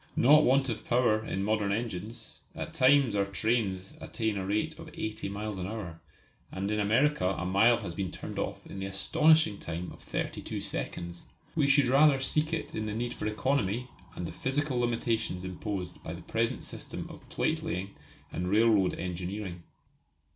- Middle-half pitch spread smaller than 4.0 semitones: No, average, 4.3 semitones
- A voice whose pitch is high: No, low, 110 Hz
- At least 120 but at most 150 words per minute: No, average, 185 wpm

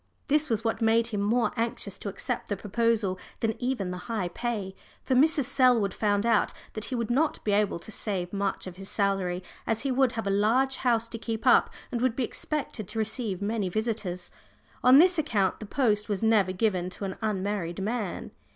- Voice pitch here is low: No, high, 220 Hz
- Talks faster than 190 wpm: Yes, fast, 205 wpm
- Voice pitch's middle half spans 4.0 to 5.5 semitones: No, average, 3.3 semitones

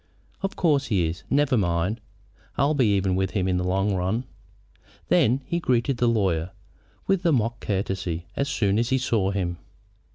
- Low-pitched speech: Yes, low, 105 Hz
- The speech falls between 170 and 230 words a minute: Yes, average, 175 wpm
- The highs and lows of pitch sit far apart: Yes, wide, 5.7 semitones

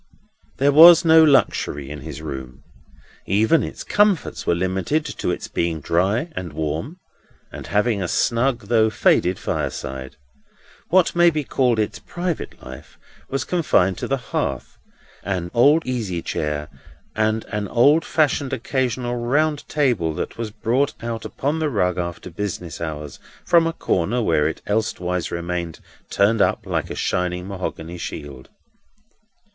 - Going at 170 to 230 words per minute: No, average, 145 wpm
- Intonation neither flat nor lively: No, wide, 8.1 semitones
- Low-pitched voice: Yes, low, 105 Hz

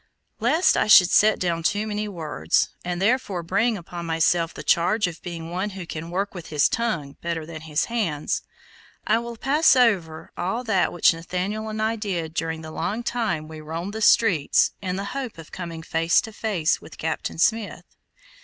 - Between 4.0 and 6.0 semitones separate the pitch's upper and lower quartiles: Yes, average, 4.9 semitones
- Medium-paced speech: Yes, average, 190 wpm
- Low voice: No, medium, 180 Hz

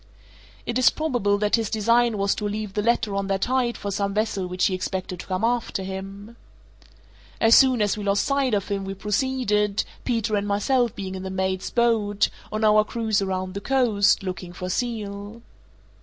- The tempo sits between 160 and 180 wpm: No, average, 190 wpm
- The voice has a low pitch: No, high, 205 Hz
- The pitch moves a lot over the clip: No, average, 3.0 semitones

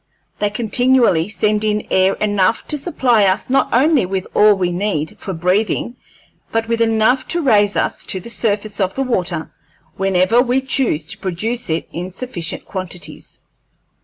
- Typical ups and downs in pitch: Yes, average, 4.2 semitones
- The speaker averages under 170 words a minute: Yes, average, 160 wpm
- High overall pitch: Yes, high, 210 Hz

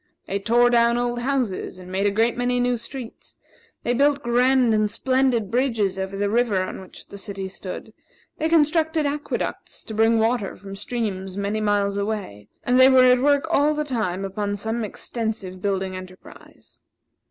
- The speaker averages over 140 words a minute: Yes, average, 175 wpm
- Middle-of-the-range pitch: No, high, 225 Hz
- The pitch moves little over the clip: No, average, 4.0 semitones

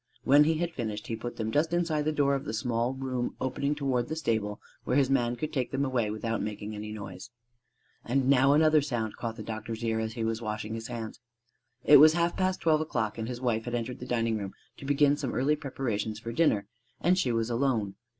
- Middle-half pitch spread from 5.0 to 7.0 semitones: No, average, 4.3 semitones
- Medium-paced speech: No, fast, 230 wpm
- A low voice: Yes, low, 120 Hz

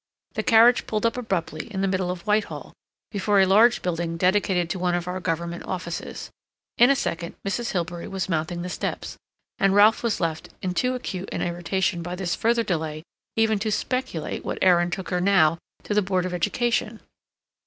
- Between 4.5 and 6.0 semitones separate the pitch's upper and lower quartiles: No, average, 3.5 semitones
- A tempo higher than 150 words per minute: Yes, average, 190 wpm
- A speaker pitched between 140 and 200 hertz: Yes, medium, 185 Hz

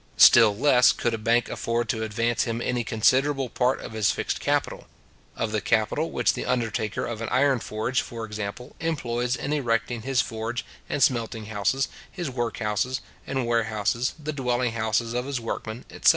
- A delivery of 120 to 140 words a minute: No, average, 180 wpm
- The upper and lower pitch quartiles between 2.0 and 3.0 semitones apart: Yes, narrow, 2.4 semitones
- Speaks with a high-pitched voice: No, low, 120 Hz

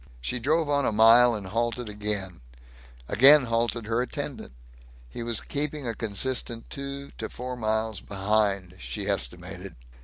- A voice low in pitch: Yes, low, 115 Hz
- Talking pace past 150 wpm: No, average, 145 wpm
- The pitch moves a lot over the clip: No, average, 3.5 semitones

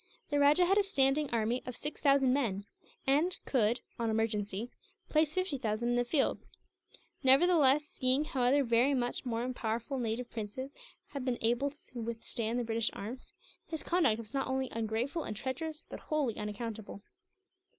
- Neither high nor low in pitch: No, very high, 255 Hz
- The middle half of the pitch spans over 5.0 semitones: No, average, 3.9 semitones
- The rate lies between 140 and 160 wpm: No, average, 170 wpm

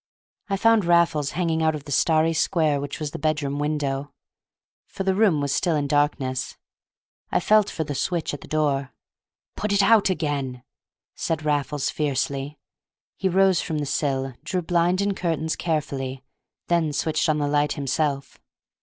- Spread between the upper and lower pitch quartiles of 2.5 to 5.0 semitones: Yes, average, 3.2 semitones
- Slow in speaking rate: No, average, 165 wpm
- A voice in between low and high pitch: Yes, medium, 155 Hz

